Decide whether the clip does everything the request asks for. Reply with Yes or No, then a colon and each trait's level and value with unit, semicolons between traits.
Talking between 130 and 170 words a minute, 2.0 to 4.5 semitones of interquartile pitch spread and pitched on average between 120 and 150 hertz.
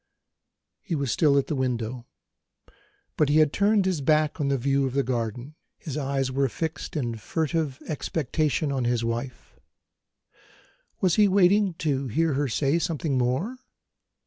Yes: average, 155 wpm; average, 3.9 semitones; medium, 140 Hz